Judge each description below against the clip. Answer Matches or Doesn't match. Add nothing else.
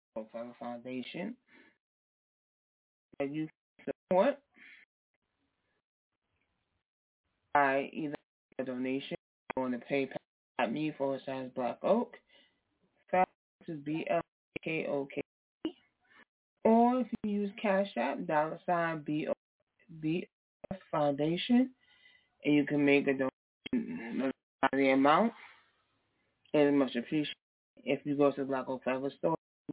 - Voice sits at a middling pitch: Matches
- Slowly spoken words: Matches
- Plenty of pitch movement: Matches